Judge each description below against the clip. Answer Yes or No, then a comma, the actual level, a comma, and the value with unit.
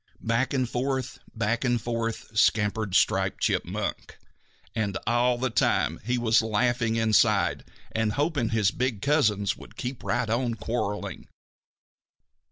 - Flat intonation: Yes, narrow, 2.3 semitones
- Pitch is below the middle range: Yes, low, 115 Hz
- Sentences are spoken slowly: Yes, slow, 130 wpm